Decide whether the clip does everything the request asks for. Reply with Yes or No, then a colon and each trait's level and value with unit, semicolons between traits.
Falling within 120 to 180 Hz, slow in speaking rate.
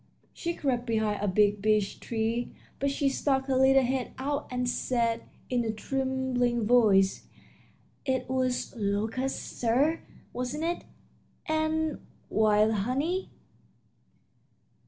No: very high, 250 Hz; slow, 115 wpm